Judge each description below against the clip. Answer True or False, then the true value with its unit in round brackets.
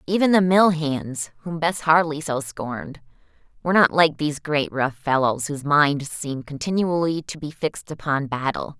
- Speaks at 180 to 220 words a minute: False (170 wpm)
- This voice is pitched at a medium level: True (150 Hz)